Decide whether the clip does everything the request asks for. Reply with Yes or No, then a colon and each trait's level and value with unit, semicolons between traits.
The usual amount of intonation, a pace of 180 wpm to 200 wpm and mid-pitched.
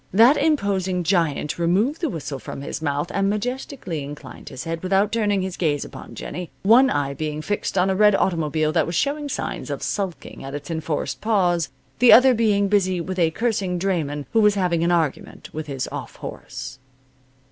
Yes: average, 5.0 semitones; average, 190 wpm; medium, 180 Hz